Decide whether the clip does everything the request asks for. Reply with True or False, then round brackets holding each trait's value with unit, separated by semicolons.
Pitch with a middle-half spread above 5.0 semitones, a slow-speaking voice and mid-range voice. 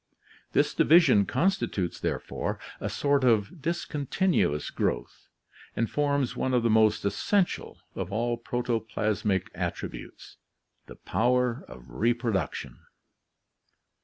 False (5.4 semitones; 105 wpm; 120 Hz)